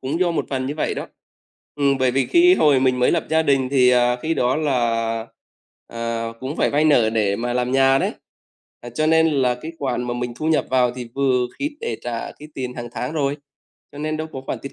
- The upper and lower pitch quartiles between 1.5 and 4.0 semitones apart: Yes, average, 3.6 semitones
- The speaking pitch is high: No, low, 135 Hz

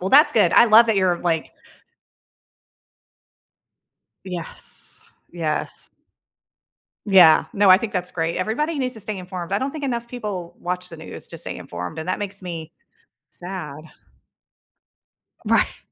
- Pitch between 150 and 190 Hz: Yes, medium, 185 Hz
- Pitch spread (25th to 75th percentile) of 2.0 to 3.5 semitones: No, average, 4.2 semitones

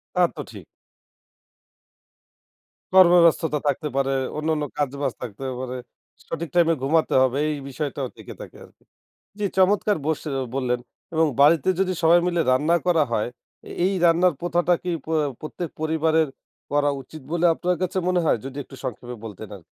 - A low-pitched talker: No, medium, 155 Hz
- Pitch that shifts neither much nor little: Yes, average, 4.1 semitones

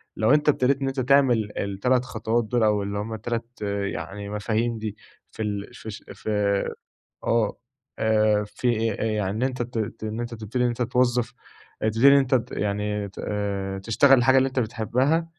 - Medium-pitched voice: No, low, 115 Hz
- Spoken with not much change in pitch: No, average, 3.2 semitones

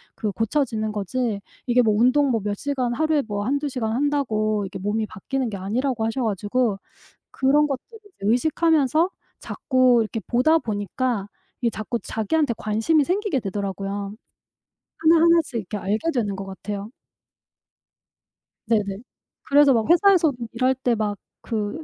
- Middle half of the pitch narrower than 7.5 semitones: Yes, average, 5.3 semitones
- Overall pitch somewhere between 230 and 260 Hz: Yes, high, 235 Hz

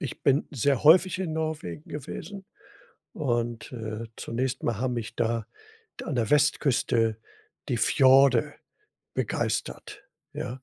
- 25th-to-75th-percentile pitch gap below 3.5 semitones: No, average, 4.2 semitones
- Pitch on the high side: No, low, 130 Hz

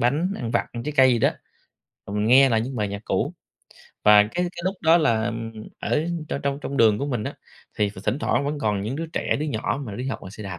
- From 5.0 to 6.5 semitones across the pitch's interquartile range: Yes, average, 5.3 semitones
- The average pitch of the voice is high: No, low, 120 Hz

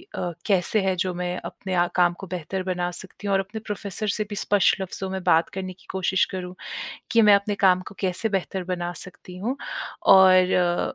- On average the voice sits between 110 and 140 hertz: No, medium, 185 Hz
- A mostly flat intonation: Yes, narrow, 1.5 semitones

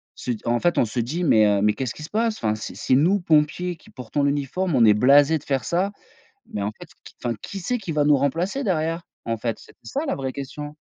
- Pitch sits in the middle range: Yes, medium, 145 Hz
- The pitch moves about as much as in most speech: No, wide, 6.3 semitones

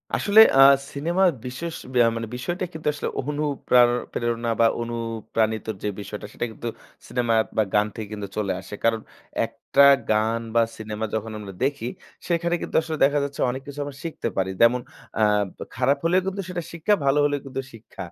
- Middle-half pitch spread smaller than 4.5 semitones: No, average, 4.8 semitones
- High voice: No, low, 125 Hz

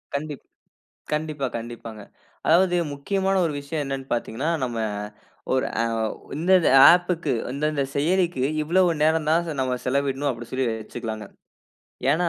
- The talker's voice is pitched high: No, medium, 145 Hz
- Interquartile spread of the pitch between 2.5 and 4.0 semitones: No, average, 4.6 semitones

